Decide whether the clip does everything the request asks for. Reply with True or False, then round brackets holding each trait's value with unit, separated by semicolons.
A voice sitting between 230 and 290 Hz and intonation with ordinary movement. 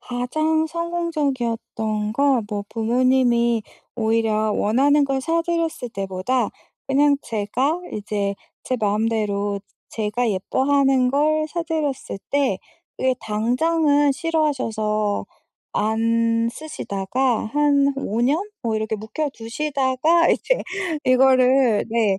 True (250 Hz; 4.7 semitones)